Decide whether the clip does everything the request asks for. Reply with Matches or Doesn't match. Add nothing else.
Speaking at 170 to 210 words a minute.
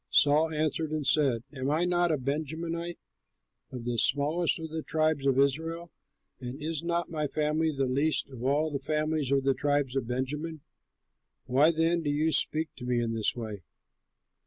Matches